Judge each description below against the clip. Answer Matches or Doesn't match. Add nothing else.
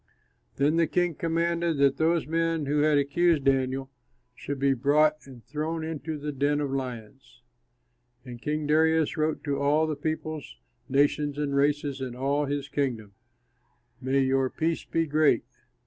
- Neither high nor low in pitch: Matches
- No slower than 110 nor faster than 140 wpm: Doesn't match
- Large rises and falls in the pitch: Doesn't match